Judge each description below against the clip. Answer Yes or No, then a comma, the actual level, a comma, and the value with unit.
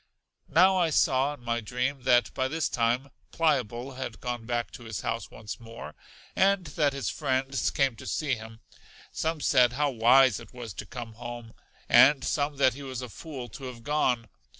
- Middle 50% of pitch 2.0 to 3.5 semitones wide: Yes, average, 3.2 semitones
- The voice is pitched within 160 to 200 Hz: No, low, 130 Hz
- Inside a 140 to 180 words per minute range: No, average, 190 wpm